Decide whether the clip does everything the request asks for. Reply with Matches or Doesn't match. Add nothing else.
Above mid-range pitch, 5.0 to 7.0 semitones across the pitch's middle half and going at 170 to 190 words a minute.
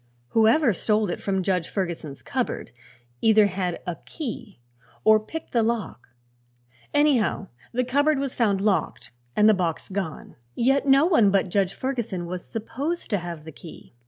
Doesn't match